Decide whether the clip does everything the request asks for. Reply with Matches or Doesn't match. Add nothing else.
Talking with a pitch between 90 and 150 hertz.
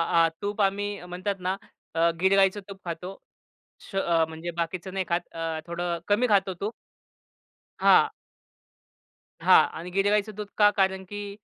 Doesn't match